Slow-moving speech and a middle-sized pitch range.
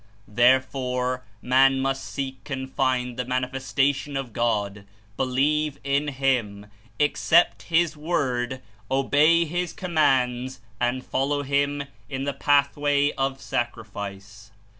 No: slow, 120 wpm; narrow, 2.3 semitones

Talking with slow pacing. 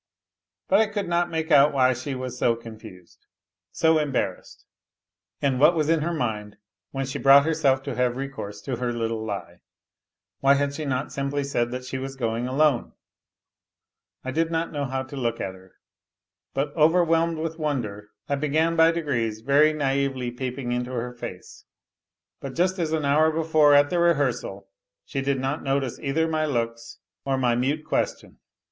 No: average, 175 wpm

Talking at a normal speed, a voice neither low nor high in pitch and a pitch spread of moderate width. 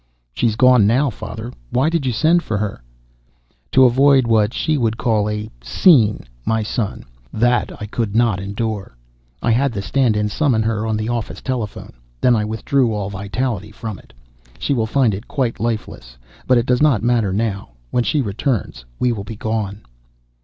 No: average, 180 wpm; low, 115 Hz; average, 3.0 semitones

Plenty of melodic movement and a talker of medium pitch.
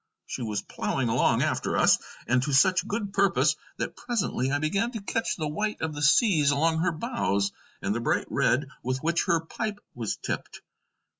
Yes: wide, 7.2 semitones; medium, 155 Hz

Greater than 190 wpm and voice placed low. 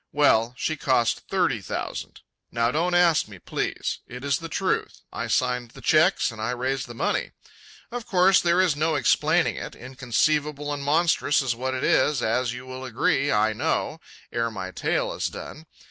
No: average, 180 wpm; low, 130 Hz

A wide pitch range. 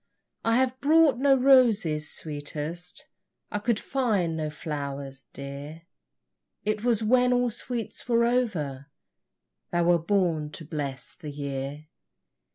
Yes: wide, 8.5 semitones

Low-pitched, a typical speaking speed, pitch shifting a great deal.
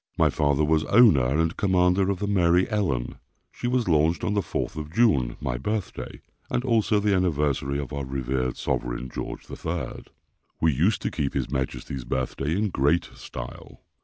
Yes: very low, 80 Hz; average, 170 wpm; wide, 6.6 semitones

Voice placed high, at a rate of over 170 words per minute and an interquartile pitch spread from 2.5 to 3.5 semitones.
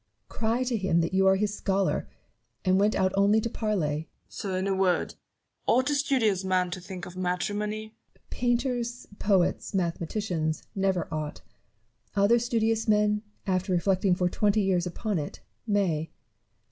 No: high, 195 Hz; average, 160 wpm; average, 3.1 semitones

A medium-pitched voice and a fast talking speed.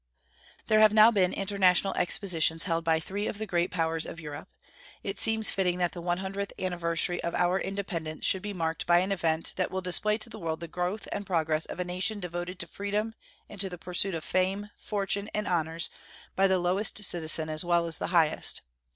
Yes: medium, 180 Hz; fast, 210 wpm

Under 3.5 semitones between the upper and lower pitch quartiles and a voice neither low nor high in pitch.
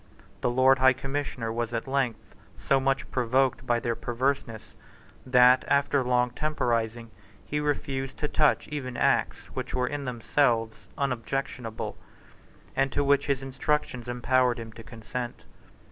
No: narrow, 2.5 semitones; low, 125 Hz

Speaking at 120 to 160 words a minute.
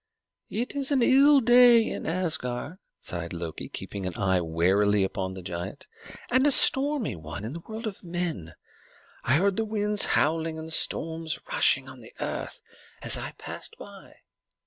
No: average, 170 wpm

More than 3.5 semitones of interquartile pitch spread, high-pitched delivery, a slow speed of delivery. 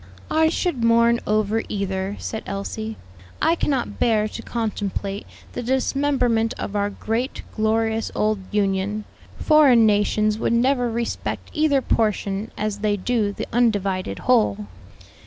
No: average, 2.7 semitones; high, 220 Hz; slow, 130 wpm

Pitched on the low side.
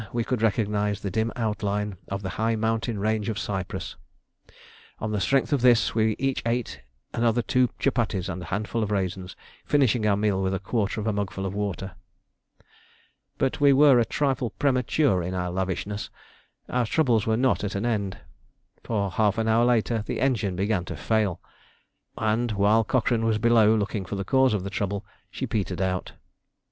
Yes: low, 110 Hz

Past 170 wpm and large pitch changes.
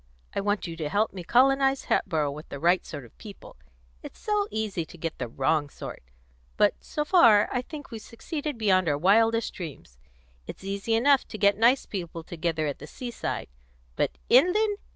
Yes: average, 185 wpm; wide, 7.2 semitones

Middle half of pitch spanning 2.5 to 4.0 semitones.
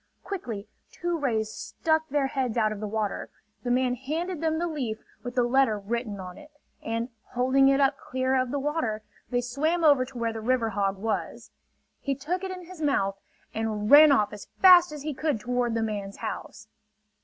No: average, 5.2 semitones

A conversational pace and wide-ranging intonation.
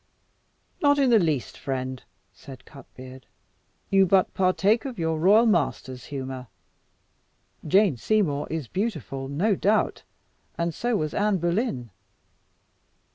No: slow, 120 wpm; wide, 7.6 semitones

